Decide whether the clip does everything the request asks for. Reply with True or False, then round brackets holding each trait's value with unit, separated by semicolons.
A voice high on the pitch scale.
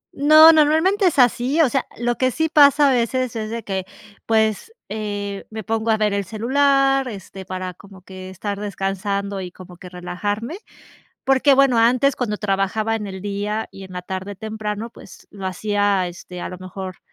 True (210 Hz)